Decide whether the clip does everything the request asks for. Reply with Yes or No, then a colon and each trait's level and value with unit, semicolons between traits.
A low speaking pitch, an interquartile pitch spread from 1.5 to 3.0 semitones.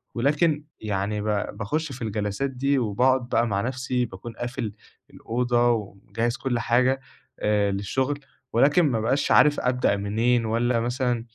No: low, 120 Hz; average, 3.5 semitones